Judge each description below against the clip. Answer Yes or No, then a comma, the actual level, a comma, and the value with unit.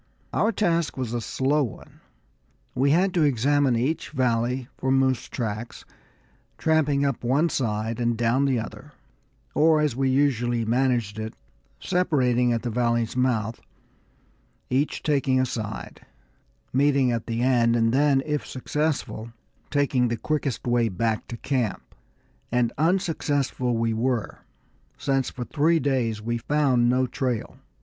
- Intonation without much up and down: No, average, 3.4 semitones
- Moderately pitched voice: No, low, 130 Hz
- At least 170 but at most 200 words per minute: No, average, 140 wpm